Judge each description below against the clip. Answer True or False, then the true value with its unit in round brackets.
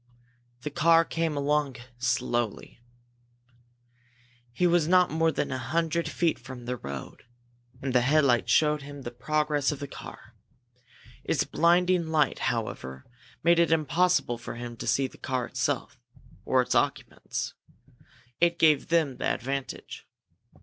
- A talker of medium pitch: True (145 Hz)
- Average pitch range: True (4.7 semitones)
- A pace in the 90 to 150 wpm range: True (140 wpm)